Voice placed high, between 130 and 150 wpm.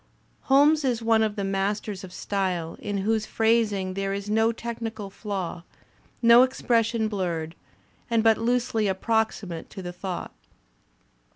Yes: high, 215 Hz; slow, 135 wpm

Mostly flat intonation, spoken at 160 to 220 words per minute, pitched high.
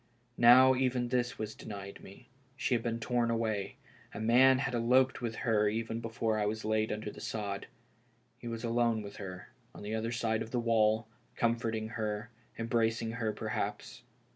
No: narrow, 1.7 semitones; average, 185 wpm; low, 115 Hz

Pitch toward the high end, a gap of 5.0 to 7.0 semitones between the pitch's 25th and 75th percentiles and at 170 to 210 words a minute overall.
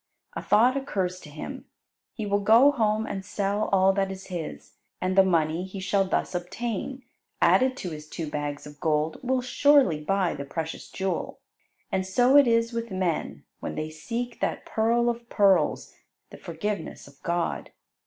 Yes: high, 195 Hz; wide, 5.4 semitones; average, 175 wpm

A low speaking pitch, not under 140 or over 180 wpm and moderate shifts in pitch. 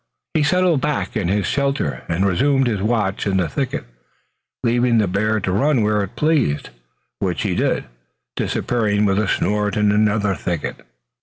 Yes: low, 105 Hz; average, 165 wpm; average, 4.1 semitones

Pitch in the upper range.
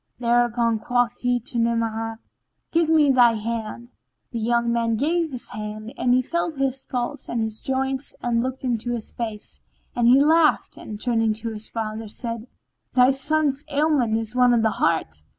Yes: high, 240 Hz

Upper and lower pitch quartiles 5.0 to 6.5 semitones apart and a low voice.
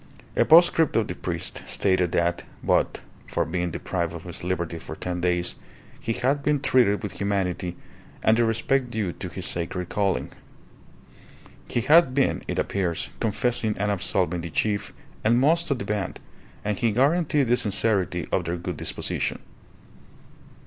Yes: wide, 5.5 semitones; low, 100 Hz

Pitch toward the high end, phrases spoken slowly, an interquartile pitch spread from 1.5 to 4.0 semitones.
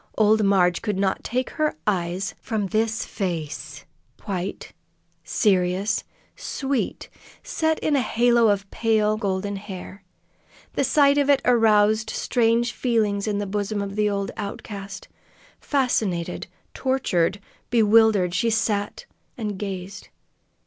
Yes: high, 210 Hz; slow, 120 wpm; average, 2.8 semitones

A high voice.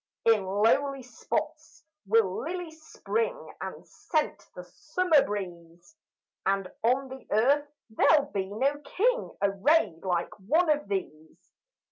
Yes: very high, 250 Hz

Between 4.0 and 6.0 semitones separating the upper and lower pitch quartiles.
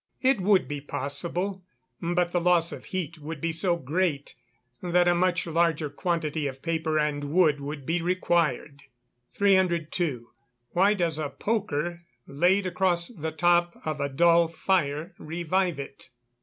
No: average, 3.0 semitones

